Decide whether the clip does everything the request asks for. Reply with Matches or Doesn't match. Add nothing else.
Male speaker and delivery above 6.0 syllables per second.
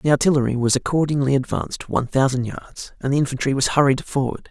Matches